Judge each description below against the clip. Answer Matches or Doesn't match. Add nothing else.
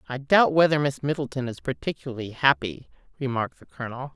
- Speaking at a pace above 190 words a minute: Doesn't match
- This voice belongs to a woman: Matches